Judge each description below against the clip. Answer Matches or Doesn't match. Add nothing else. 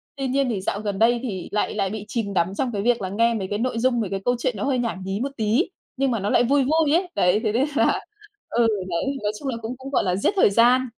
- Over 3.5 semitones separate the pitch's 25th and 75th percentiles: Matches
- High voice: Matches